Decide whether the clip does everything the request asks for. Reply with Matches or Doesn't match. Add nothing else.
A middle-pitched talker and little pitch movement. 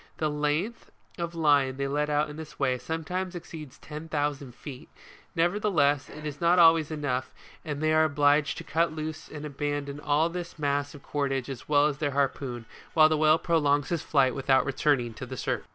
Matches